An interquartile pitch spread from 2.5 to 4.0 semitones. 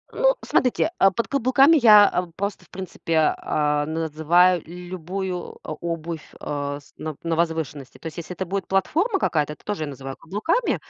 No: average, 4.6 semitones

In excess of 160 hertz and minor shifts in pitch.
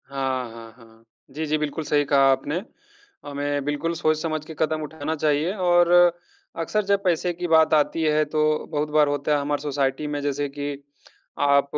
No: medium, 150 Hz; narrow, 1.9 semitones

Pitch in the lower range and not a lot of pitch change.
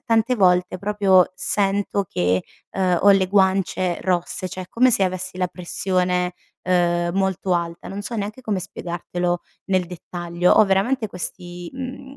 No: medium, 185 Hz; narrow, 2.1 semitones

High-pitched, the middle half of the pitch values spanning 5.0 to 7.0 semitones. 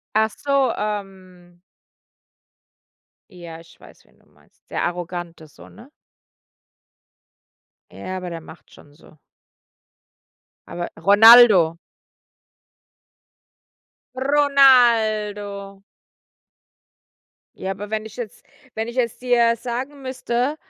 Yes: high, 210 Hz; average, 5.3 semitones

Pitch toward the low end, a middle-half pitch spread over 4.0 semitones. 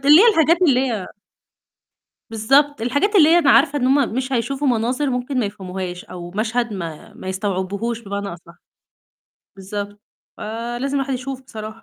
No: high, 240 Hz; wide, 5.5 semitones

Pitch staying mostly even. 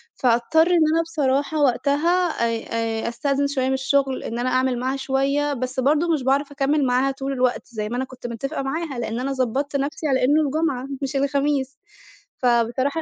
Yes: narrow, 2.2 semitones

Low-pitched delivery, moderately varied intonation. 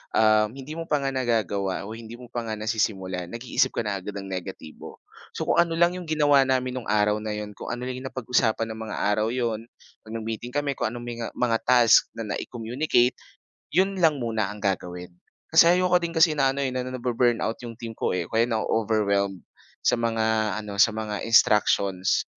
Yes: low, 115 Hz; average, 3.4 semitones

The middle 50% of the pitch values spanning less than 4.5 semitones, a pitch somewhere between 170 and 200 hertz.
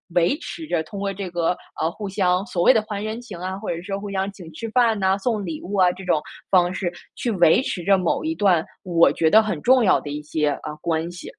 Yes: average, 3.4 semitones; high, 190 Hz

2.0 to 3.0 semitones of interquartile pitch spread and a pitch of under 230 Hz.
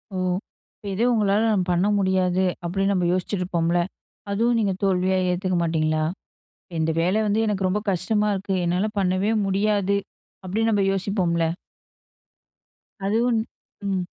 Yes: narrow, 2.4 semitones; high, 190 Hz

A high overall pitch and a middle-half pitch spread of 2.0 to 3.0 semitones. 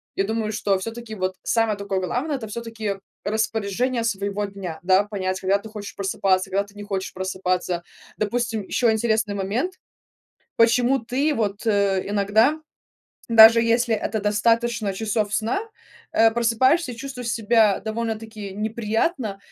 Yes: high, 220 Hz; narrow, 2.5 semitones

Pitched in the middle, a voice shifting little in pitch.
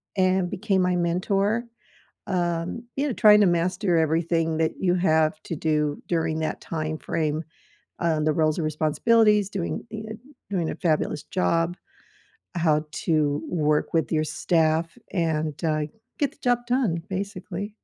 No: medium, 170 Hz; average, 3.4 semitones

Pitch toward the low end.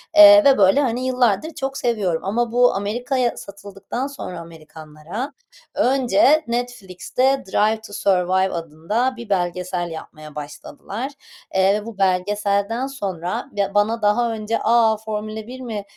No: high, 210 Hz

